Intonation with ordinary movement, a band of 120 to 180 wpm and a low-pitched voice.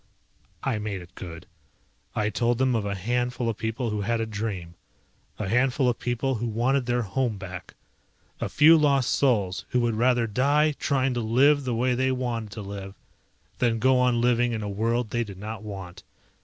No: average, 3.2 semitones; average, 195 wpm; low, 115 Hz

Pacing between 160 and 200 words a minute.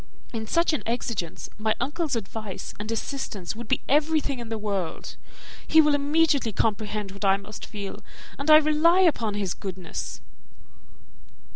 No: average, 150 wpm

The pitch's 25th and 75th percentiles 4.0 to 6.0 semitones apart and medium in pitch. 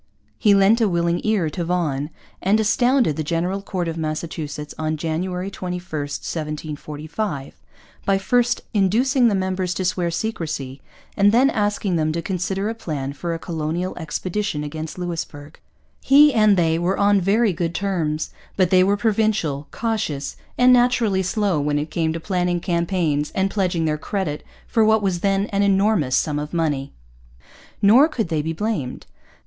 Yes: average, 4.5 semitones; medium, 180 Hz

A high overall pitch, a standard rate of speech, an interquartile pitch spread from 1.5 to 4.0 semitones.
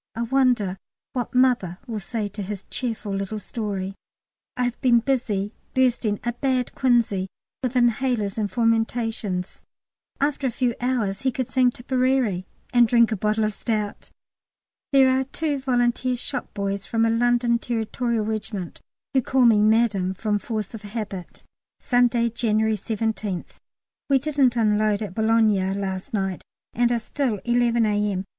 Yes: high, 225 Hz; average, 150 wpm; average, 3.0 semitones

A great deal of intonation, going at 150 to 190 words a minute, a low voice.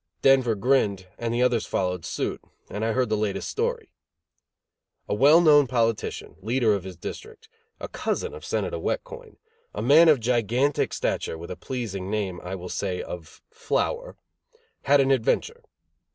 Yes: wide, 7.0 semitones; average, 165 wpm; low, 120 Hz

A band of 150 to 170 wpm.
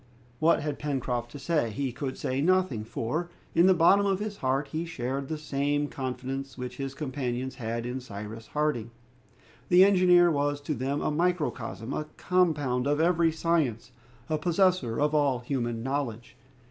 Yes: average, 160 wpm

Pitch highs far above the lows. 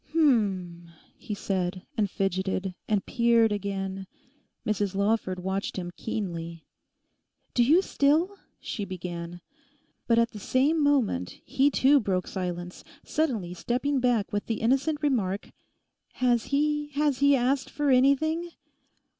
Yes: wide, 6.7 semitones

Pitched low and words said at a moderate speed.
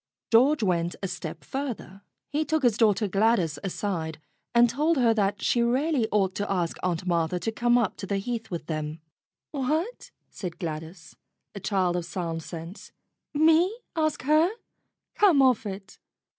No: high, 205 Hz; average, 160 wpm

